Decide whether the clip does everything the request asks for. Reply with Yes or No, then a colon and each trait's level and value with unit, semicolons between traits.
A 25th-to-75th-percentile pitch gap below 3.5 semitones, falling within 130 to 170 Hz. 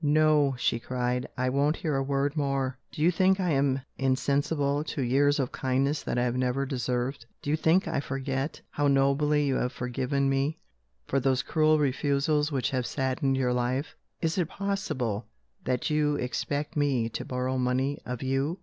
Yes: narrow, 2.4 semitones; low, 135 Hz